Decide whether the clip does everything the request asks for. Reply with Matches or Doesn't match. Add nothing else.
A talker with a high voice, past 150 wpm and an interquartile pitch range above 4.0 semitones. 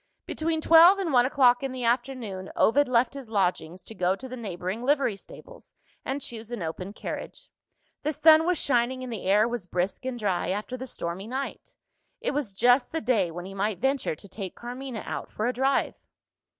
Matches